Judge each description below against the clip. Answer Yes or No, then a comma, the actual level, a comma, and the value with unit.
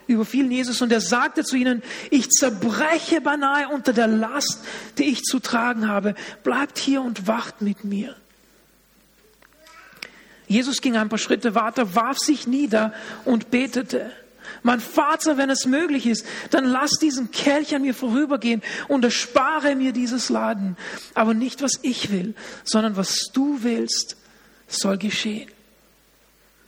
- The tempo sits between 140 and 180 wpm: Yes, average, 145 wpm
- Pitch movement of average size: Yes, average, 3.8 semitones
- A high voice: Yes, very high, 250 Hz